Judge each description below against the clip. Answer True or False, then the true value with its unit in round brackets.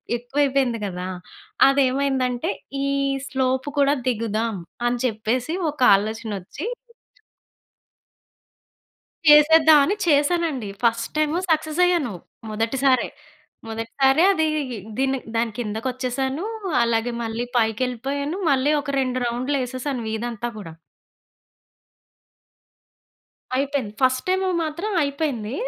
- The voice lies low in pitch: False (260 Hz)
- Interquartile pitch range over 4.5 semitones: False (3.8 semitones)